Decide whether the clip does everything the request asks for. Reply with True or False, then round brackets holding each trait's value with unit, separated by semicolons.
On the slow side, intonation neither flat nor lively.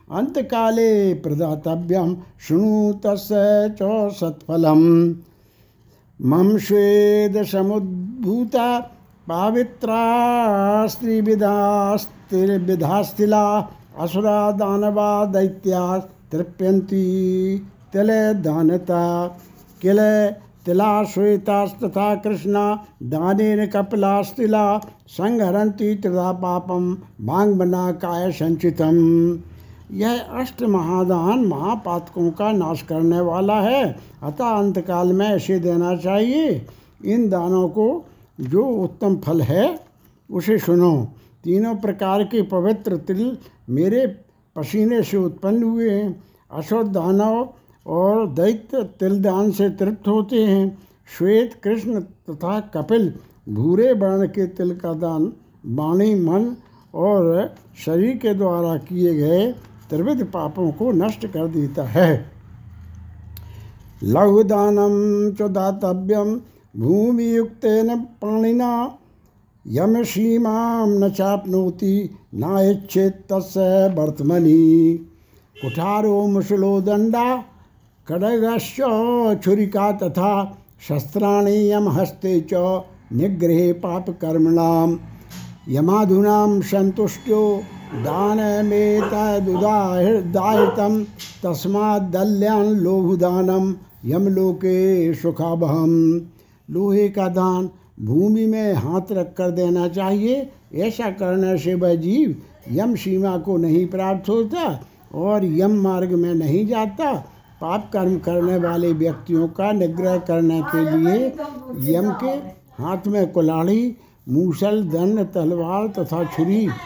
True (90 wpm; 3.6 semitones)